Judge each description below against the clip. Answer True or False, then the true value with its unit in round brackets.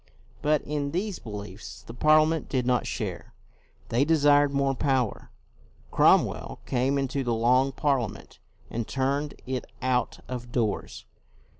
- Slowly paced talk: True (130 wpm)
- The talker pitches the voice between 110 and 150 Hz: True (135 Hz)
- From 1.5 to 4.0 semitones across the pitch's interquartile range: True (2.8 semitones)